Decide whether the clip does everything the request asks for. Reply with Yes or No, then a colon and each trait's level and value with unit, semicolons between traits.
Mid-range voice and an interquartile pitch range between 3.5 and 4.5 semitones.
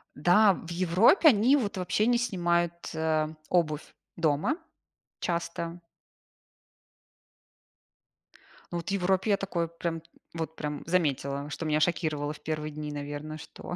No: medium, 170 Hz; average, 3.1 semitones